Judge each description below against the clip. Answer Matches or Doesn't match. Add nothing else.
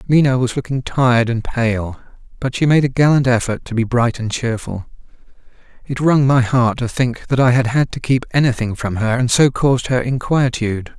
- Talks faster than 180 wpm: Matches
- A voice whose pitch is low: Matches